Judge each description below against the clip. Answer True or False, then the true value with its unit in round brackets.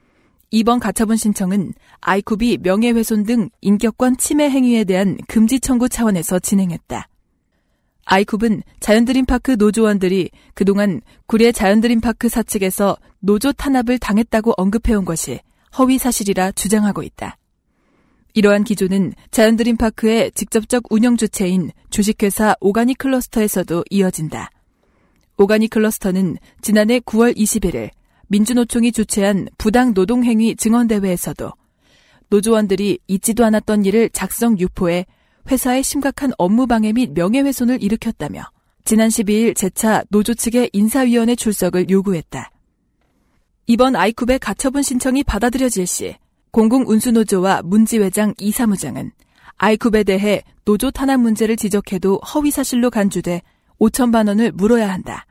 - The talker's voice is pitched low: False (220 Hz)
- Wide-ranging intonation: False (3.3 semitones)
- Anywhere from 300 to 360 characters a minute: True (325 characters per minute)